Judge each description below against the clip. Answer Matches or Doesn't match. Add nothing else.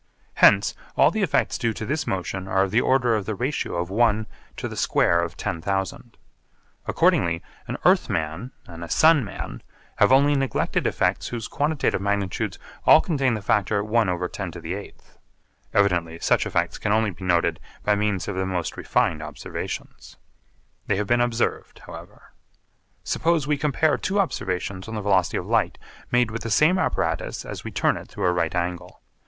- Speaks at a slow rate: Doesn't match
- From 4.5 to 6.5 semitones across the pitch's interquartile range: Matches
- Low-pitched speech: Matches